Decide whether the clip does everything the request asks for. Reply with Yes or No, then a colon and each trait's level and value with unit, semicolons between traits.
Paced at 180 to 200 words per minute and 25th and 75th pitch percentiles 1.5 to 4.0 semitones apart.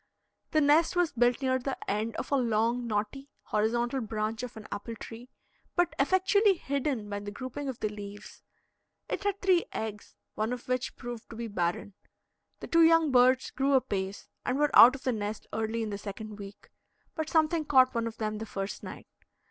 No: average, 195 wpm; average, 4.5 semitones